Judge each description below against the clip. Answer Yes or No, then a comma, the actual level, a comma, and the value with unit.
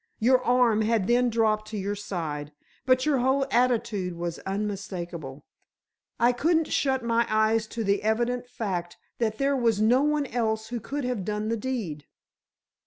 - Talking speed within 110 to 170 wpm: Yes, average, 165 wpm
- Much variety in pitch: No, average, 3.5 semitones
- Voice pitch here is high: Yes, high, 225 Hz